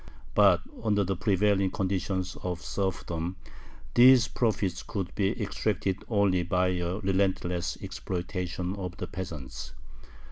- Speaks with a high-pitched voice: No, very low, 95 Hz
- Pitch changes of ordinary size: No, narrow, 2.0 semitones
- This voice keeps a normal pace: No, slow, 115 wpm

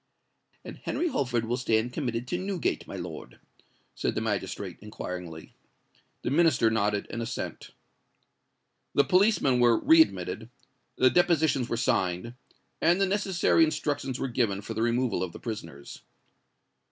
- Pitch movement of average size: No, wide, 6.4 semitones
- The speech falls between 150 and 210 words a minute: No, average, 140 wpm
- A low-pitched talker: Yes, low, 125 Hz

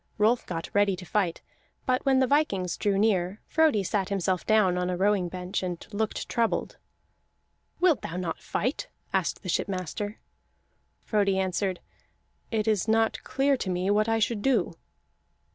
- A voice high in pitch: Yes, high, 205 Hz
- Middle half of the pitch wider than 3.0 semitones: Yes, average, 3.5 semitones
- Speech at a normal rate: Yes, average, 160 wpm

